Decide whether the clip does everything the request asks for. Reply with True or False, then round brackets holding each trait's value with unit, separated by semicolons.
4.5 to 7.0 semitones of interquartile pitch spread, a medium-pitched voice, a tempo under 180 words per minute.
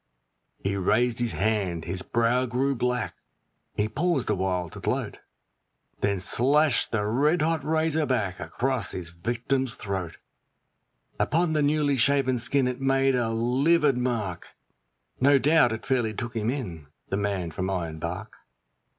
False (5.6 semitones; 120 Hz; 140 wpm)